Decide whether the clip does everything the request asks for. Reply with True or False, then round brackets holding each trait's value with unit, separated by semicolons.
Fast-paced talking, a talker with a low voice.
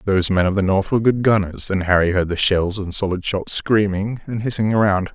True (235 wpm; 100 Hz)